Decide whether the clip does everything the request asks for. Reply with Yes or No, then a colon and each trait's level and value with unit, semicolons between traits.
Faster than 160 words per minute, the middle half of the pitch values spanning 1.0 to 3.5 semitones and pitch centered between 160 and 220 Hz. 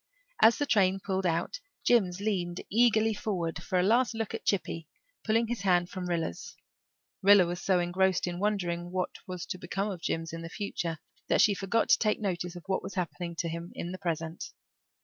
Yes: average, 200 wpm; average, 2.9 semitones; medium, 185 Hz